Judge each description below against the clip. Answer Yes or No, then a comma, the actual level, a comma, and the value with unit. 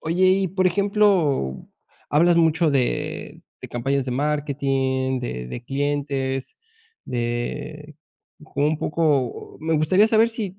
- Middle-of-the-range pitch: Yes, medium, 150 Hz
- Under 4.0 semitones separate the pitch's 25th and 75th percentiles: No, average, 4.6 semitones